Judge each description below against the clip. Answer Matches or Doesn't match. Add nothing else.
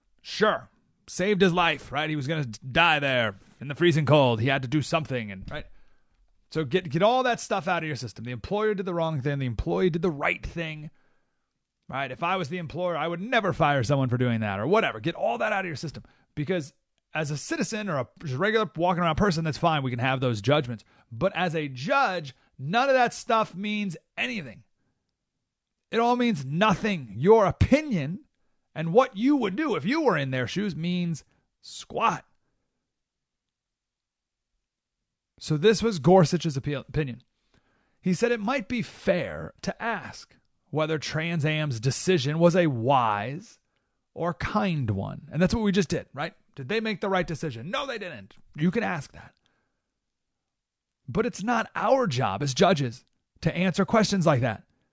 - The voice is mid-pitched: Matches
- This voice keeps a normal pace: Matches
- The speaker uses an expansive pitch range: Matches